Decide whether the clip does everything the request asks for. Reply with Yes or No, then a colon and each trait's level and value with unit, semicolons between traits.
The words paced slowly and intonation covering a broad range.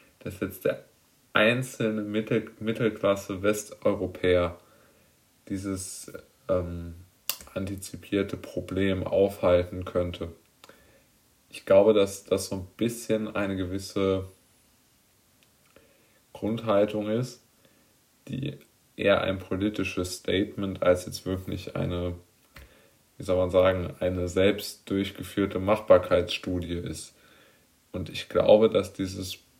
No: slow, 95 wpm; narrow, 2.5 semitones